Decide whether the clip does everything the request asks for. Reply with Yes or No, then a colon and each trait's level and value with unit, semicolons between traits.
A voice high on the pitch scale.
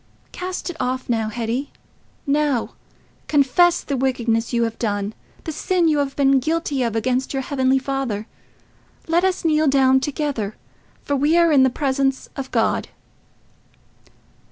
Yes: very high, 270 Hz